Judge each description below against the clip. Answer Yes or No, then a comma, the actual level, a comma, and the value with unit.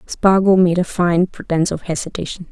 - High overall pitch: No, medium, 175 Hz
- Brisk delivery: No, average, 165 wpm